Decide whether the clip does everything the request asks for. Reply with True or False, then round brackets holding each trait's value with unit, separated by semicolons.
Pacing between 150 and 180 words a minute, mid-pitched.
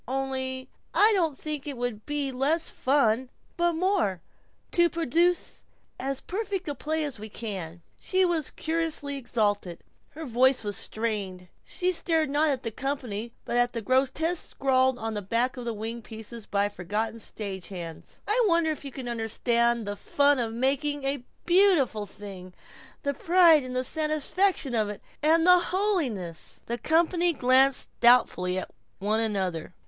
False (155 wpm; 260 Hz)